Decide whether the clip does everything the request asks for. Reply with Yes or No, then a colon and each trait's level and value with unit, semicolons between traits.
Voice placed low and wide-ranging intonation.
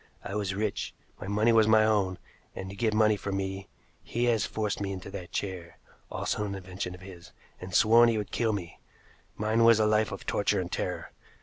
No: low, 100 Hz; narrow, 2.4 semitones